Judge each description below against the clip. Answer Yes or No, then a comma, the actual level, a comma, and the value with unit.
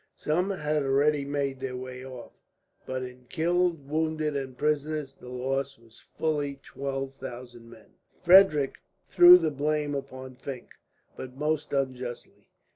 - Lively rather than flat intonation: No, average, 2.9 semitones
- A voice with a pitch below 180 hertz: Yes, medium, 140 Hz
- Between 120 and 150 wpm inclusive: Yes, slow, 135 wpm